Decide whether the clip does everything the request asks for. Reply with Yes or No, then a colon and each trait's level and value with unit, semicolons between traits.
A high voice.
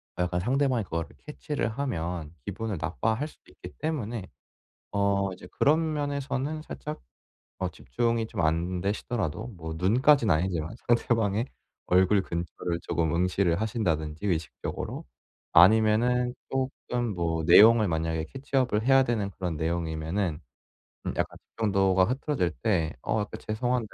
No: low, 100 Hz